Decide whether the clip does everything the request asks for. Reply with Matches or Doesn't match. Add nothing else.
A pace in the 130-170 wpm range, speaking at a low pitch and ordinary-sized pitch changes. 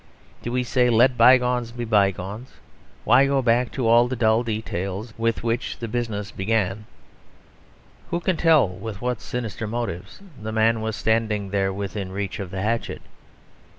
Matches